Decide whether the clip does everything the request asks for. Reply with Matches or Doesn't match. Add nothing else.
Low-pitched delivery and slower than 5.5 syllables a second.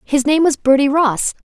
Doesn't match